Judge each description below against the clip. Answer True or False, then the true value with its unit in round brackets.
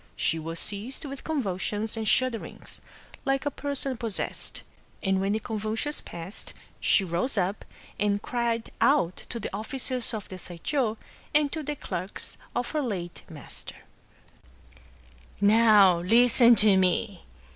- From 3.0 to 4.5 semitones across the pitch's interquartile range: False (5.2 semitones)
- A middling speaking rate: True (145 wpm)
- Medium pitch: False (215 Hz)